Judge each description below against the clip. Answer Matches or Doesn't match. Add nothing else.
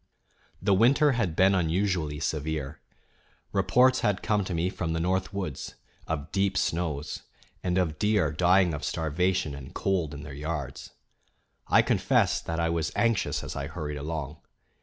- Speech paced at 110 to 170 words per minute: Matches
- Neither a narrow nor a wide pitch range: Matches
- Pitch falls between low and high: Doesn't match